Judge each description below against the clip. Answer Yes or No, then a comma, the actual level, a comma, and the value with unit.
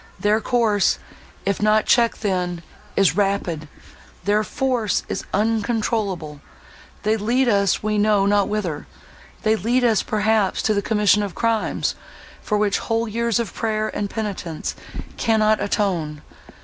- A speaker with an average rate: No, slow, 125 wpm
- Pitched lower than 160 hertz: No, high, 210 Hz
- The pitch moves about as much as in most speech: No, narrow, 2.0 semitones